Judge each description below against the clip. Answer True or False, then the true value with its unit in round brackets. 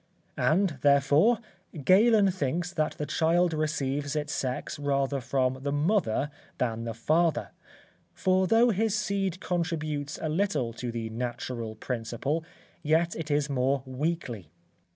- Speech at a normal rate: False (130 wpm)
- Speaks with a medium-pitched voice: True (150 Hz)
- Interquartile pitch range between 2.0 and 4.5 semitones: False (5.0 semitones)